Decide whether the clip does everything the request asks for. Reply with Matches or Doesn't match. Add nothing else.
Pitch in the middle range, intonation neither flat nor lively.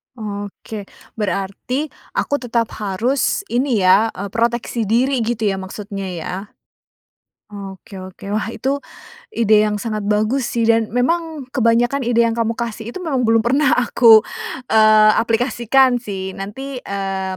Doesn't match